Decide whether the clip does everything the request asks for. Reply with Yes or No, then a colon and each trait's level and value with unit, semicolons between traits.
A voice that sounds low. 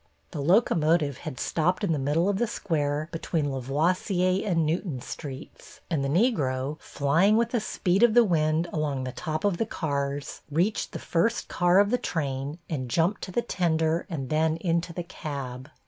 No: medium, 160 Hz